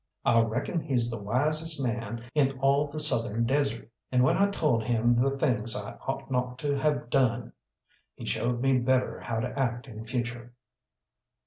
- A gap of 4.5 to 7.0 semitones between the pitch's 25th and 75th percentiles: No, average, 2.7 semitones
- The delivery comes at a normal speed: Yes, average, 175 wpm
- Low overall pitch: Yes, low, 125 Hz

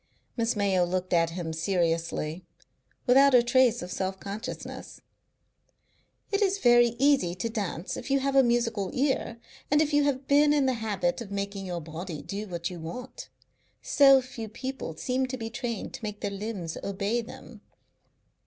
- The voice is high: Yes, high, 220 Hz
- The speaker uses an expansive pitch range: Yes, wide, 6.0 semitones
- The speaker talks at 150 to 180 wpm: Yes, average, 170 wpm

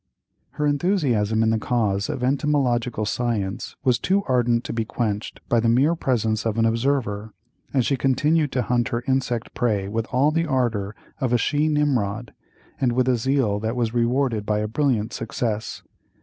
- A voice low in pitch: Yes, low, 120 Hz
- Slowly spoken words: No, average, 175 wpm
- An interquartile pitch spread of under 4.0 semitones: Yes, average, 3.3 semitones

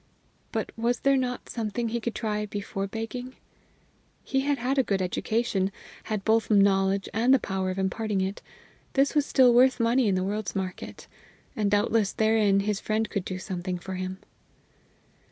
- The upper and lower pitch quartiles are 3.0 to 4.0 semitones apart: Yes, average, 3.6 semitones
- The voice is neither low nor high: No, high, 215 Hz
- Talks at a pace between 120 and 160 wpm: No, average, 175 wpm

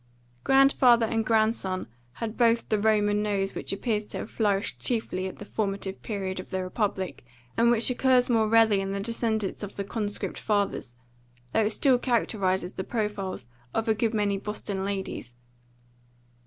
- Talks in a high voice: Yes, high, 210 Hz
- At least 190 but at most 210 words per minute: No, average, 165 wpm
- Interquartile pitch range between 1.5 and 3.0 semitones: Yes, narrow, 2.5 semitones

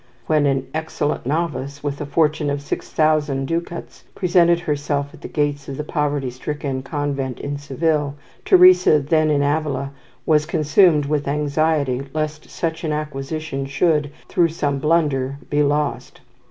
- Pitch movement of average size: No, narrow, 1.9 semitones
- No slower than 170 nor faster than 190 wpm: No, average, 150 wpm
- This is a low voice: No, medium, 150 Hz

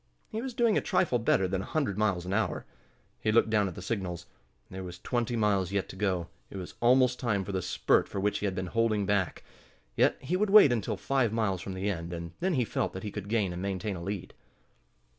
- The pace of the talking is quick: Yes, fast, 240 wpm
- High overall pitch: No, low, 100 Hz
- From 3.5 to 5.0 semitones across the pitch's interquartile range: Yes, average, 4.0 semitones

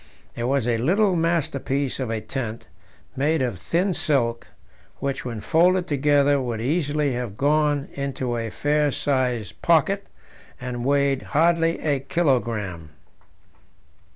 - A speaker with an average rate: No, slow, 125 wpm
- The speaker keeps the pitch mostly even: No, average, 4.1 semitones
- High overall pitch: No, medium, 140 Hz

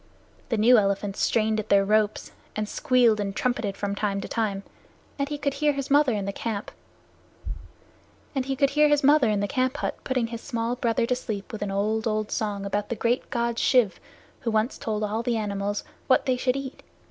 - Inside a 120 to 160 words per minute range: No, average, 180 wpm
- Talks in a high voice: Yes, high, 225 Hz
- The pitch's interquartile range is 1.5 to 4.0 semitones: Yes, average, 3.7 semitones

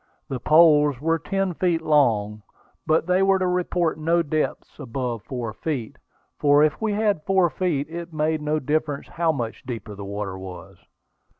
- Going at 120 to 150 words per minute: No, average, 170 wpm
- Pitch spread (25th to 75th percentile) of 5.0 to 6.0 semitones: Yes, wide, 5.6 semitones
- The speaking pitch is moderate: Yes, medium, 155 Hz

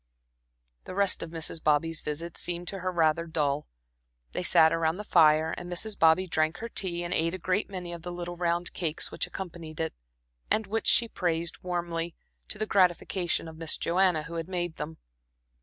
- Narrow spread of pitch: Yes, narrow, 2.1 semitones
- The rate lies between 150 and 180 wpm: No, average, 190 wpm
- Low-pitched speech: No, medium, 170 Hz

